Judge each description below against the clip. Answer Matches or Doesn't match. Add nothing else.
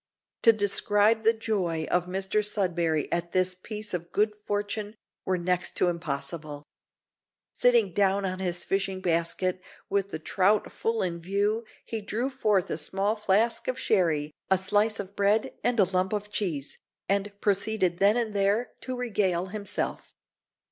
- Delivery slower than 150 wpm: Doesn't match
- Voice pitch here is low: Doesn't match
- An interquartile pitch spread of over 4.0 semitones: Doesn't match